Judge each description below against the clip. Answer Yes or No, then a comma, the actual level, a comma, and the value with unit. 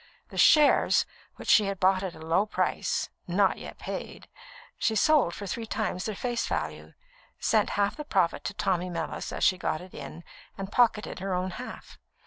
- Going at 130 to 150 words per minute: No, average, 185 wpm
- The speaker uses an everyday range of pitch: Yes, average, 3.3 semitones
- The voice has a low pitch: No, high, 195 Hz